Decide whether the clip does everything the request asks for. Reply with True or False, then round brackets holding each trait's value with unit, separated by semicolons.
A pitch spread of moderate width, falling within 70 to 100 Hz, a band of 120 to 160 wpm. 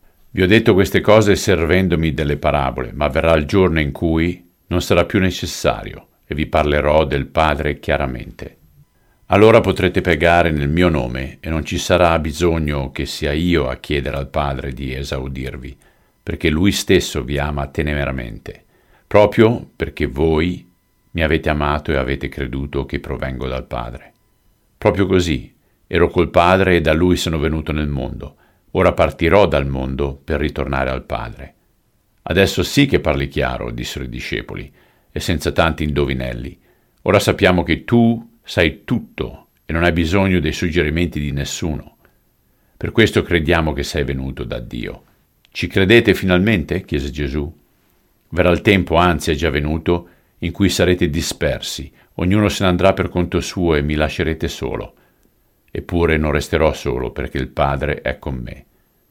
True (4.0 semitones; 80 Hz; 155 wpm)